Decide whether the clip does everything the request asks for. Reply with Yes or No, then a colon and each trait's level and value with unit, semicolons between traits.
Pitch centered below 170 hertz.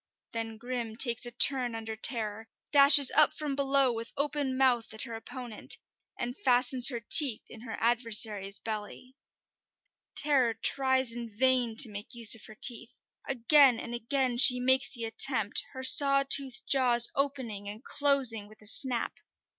No: high, 245 Hz